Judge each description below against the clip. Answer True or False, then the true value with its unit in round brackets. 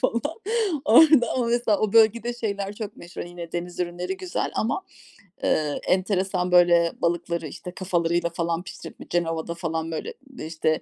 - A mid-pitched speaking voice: True (180 Hz)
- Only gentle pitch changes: False (3.4 semitones)